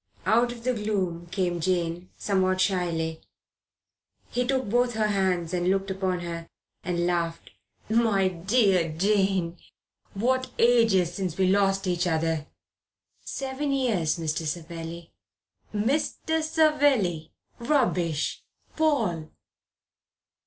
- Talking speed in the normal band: No, slow, 110 wpm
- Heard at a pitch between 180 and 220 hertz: Yes, high, 190 Hz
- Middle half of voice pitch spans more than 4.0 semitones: Yes, average, 5.3 semitones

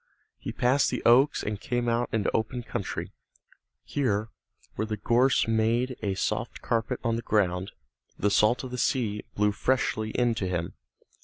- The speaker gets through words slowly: No, average, 165 wpm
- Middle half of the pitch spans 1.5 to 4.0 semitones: Yes, average, 2.8 semitones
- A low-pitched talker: Yes, low, 115 Hz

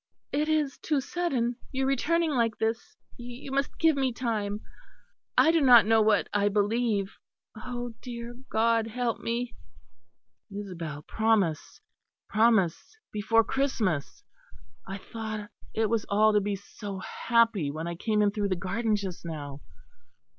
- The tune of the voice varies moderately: Yes, average, 3.3 semitones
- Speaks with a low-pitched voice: No, high, 225 Hz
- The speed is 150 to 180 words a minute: No, average, 140 wpm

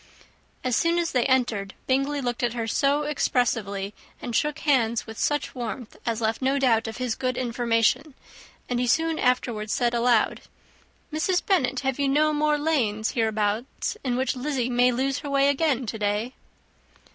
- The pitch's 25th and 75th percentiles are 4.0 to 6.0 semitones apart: No, average, 3.5 semitones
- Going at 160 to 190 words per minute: Yes, average, 170 wpm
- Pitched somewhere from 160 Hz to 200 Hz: No, very high, 250 Hz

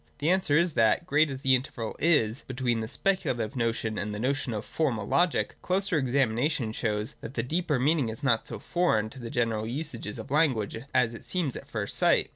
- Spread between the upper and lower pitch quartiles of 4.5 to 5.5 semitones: Yes, average, 5.2 semitones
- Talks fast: Yes, fast, 210 wpm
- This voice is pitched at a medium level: No, low, 125 Hz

